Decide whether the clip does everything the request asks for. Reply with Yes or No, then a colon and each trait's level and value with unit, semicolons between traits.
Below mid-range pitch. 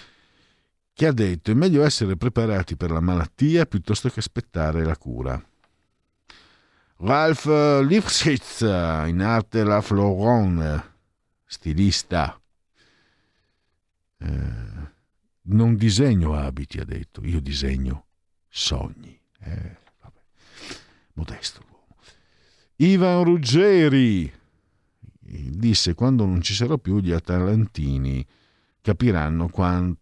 Yes: very low, 95 Hz